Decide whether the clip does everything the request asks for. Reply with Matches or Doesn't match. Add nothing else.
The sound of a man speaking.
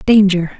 Doesn't match